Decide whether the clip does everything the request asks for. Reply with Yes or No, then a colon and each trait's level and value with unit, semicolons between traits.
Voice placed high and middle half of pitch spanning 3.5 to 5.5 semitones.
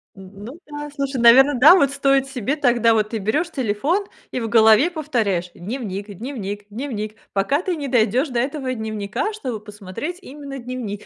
Yes: high, 245 Hz; average, 5.0 semitones